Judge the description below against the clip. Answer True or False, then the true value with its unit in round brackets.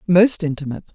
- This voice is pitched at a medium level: True (170 Hz)